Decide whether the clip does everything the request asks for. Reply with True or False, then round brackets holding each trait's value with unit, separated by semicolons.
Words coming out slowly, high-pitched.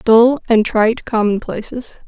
True (115 wpm; 225 Hz)